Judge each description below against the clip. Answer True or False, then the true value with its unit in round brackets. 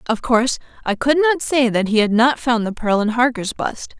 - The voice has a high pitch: True (240 Hz)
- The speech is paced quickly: True (240 wpm)